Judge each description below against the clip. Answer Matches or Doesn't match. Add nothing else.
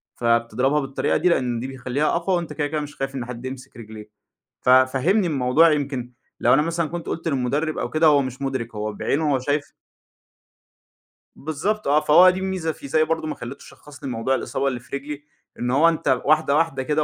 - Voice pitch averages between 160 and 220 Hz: Doesn't match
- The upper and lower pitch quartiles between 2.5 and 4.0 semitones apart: Matches